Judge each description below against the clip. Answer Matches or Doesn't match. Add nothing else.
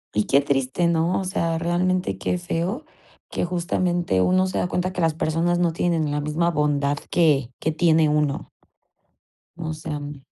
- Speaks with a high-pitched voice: Doesn't match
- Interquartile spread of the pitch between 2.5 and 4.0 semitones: Matches